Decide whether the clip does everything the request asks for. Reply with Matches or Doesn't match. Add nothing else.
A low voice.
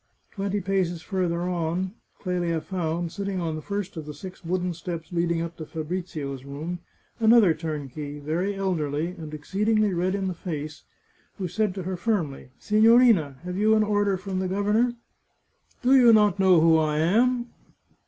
Doesn't match